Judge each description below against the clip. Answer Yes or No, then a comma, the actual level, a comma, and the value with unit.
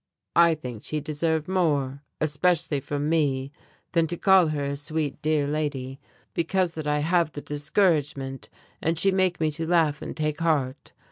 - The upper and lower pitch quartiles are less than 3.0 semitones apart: Yes, narrow, 2.5 semitones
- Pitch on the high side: No, medium, 155 Hz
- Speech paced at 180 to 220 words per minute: No, average, 165 wpm